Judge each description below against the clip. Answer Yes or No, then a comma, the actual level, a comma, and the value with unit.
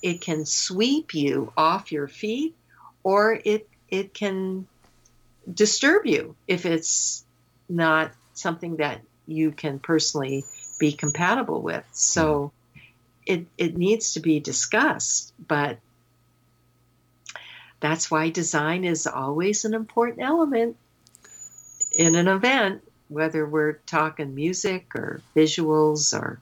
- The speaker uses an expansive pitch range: No, average, 4.6 semitones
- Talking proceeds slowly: Yes, slow, 115 wpm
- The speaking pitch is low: No, medium, 160 Hz